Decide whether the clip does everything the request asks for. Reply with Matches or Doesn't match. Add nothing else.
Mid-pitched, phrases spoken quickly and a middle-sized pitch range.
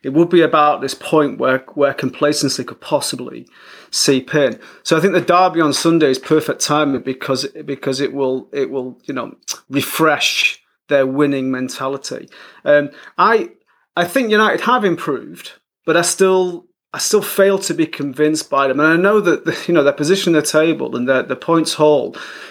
Doesn't match